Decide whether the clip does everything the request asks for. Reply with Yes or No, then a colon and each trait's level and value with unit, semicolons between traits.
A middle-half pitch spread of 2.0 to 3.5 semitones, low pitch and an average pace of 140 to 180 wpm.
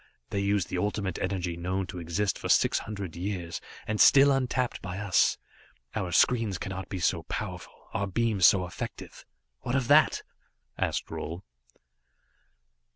Yes: average, 3.1 semitones; very low, 95 Hz; average, 150 wpm